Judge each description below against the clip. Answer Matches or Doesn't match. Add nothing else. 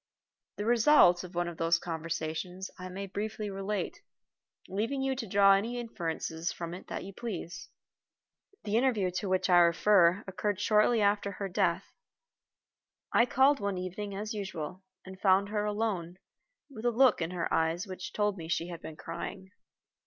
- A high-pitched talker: Matches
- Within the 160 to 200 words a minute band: Matches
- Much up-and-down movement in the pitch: Doesn't match